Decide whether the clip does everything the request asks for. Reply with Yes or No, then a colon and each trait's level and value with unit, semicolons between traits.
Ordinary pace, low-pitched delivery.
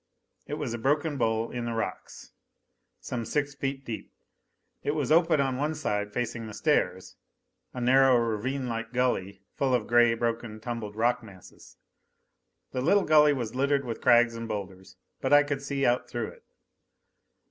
Yes: average, 165 wpm; low, 120 Hz